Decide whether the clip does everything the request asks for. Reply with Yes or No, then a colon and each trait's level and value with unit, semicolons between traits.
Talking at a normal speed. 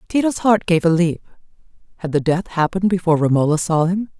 Yes: average, 170 wpm